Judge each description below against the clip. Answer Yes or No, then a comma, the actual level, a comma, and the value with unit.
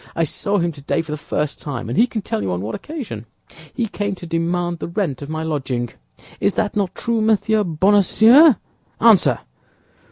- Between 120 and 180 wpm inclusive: No, average, 190 wpm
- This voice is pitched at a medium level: Yes, medium, 175 Hz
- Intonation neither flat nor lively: No, wide, 5.9 semitones